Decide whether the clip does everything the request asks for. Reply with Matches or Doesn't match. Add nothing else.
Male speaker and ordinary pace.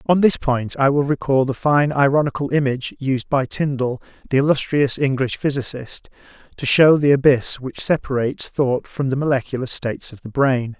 Matches